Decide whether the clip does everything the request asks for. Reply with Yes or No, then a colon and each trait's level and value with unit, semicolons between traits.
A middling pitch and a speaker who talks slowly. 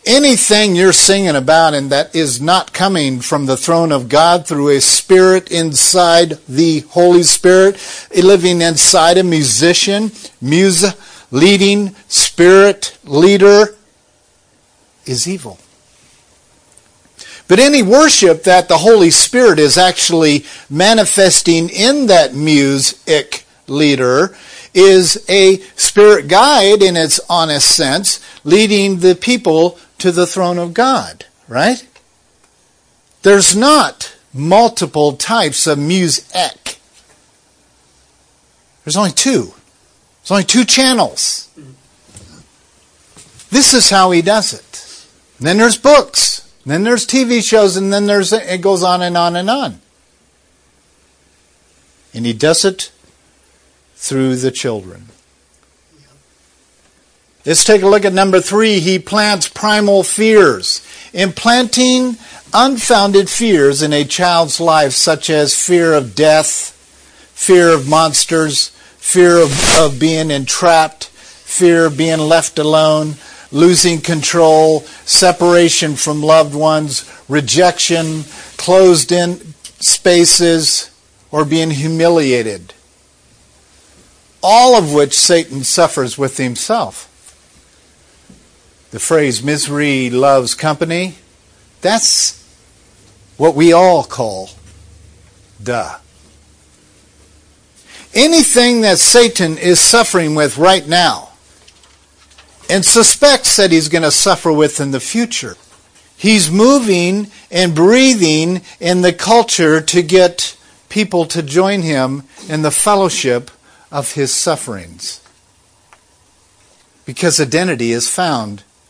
Yes: medium, 165 Hz; slow, 110 wpm